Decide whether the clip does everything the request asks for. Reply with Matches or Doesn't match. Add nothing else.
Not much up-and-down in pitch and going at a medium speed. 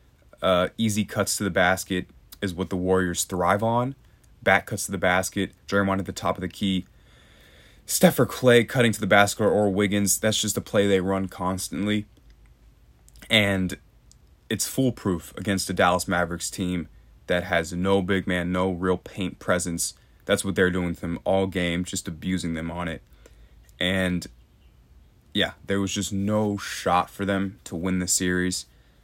Matches